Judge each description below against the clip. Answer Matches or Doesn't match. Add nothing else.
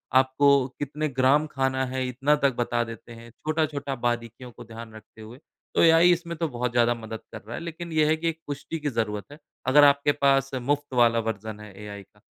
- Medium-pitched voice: Doesn't match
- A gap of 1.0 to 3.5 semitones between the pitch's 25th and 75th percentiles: Doesn't match